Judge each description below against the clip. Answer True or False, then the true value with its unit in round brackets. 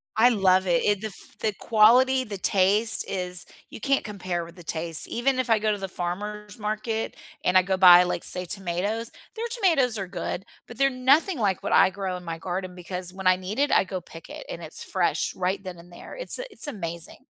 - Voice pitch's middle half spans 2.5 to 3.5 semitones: False (4.0 semitones)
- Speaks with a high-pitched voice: True (195 Hz)